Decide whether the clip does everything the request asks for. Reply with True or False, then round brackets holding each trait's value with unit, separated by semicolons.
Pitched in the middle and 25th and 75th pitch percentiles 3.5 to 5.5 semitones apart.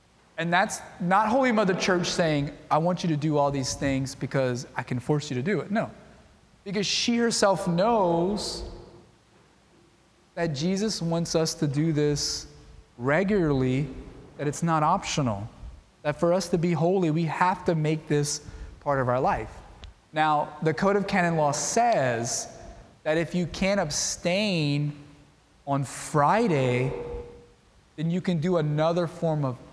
True (155 Hz; 4.2 semitones)